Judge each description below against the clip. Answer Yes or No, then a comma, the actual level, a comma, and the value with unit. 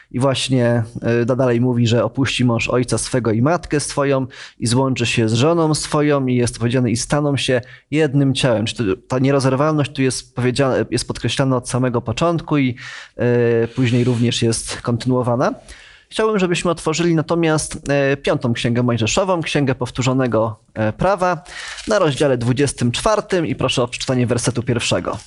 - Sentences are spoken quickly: No, average, 145 wpm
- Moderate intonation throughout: Yes, average, 3.4 semitones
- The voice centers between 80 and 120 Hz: No, low, 130 Hz